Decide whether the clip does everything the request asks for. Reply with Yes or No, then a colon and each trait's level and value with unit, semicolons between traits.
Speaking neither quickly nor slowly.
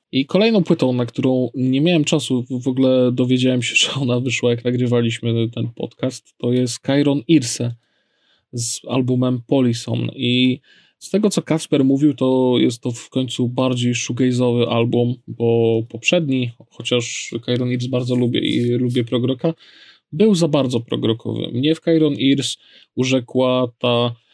Yes: average, 150 wpm